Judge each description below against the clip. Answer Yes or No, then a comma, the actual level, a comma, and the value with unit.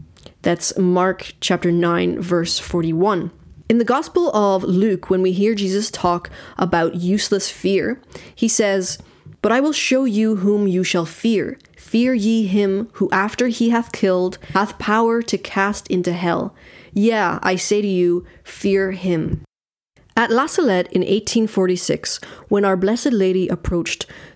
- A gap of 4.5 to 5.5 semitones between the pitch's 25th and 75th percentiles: No, average, 3.3 semitones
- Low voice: No, high, 195 Hz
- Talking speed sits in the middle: Yes, average, 150 wpm